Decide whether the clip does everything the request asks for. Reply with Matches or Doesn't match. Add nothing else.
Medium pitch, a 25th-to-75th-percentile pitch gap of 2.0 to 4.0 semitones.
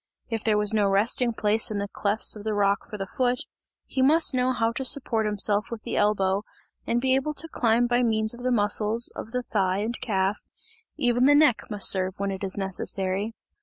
Doesn't match